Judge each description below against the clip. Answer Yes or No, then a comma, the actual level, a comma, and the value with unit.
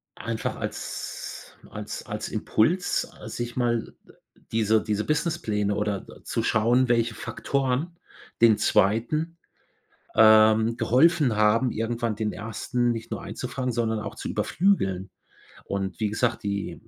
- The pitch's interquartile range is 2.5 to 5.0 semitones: Yes, average, 2.8 semitones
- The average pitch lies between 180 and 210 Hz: No, low, 115 Hz